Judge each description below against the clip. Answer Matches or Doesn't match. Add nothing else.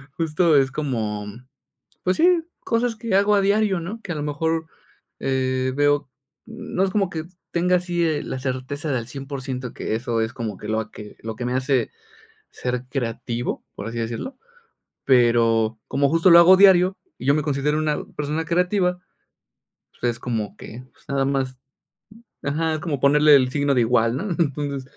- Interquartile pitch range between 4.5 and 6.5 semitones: Matches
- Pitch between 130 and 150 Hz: Matches